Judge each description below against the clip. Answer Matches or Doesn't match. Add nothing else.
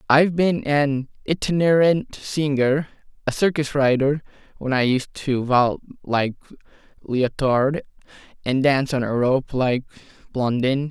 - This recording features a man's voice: Matches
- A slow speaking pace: Matches